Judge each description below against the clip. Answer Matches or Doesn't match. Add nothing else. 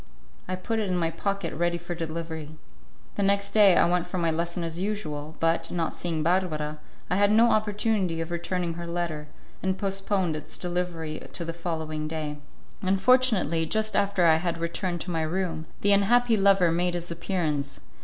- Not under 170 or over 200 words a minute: Matches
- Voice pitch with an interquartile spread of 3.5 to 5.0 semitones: Doesn't match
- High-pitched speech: Doesn't match